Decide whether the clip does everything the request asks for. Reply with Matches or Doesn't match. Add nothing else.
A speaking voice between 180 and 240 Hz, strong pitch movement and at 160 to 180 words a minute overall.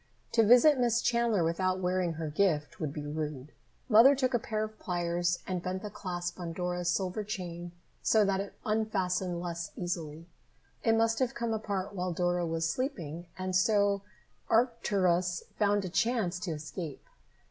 Doesn't match